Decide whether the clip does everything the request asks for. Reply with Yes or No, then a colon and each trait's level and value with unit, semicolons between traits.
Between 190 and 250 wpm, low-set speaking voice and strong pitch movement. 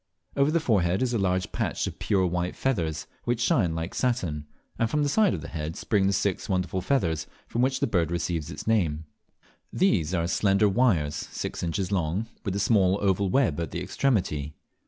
Yes: average, 200 wpm; very low, 95 Hz; wide, 5.8 semitones